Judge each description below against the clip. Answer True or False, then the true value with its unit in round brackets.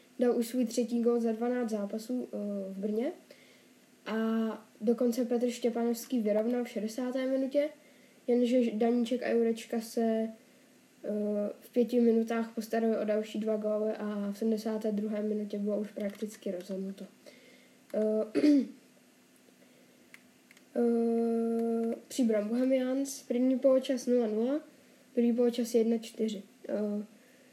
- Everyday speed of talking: False (100 wpm)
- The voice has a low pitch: False (230 Hz)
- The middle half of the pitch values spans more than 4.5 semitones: False (2.6 semitones)